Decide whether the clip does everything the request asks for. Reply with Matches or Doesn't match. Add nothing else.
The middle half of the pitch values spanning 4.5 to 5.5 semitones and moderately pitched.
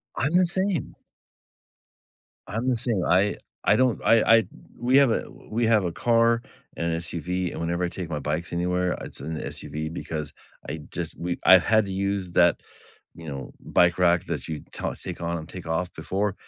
Doesn't match